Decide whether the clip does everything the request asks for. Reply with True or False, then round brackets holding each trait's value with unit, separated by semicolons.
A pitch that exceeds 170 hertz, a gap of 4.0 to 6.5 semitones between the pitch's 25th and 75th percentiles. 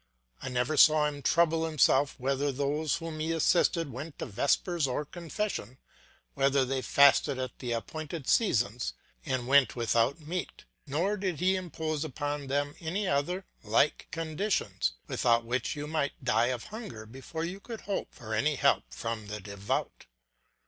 False (145 Hz; 4.5 semitones)